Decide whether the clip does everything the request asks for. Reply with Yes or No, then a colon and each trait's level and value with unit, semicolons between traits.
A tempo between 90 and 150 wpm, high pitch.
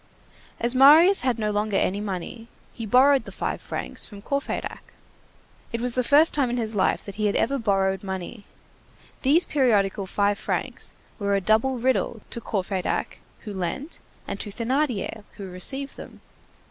No: average, 165 wpm; high, 220 Hz